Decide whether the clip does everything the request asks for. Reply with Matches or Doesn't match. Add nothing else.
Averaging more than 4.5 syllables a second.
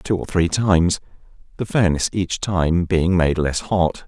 Doesn't match